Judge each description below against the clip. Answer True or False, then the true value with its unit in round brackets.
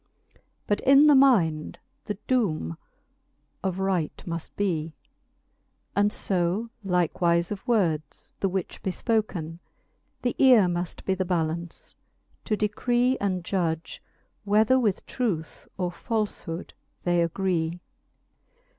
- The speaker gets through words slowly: True (115 wpm)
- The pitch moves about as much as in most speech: True (4.0 semitones)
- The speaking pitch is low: False (190 Hz)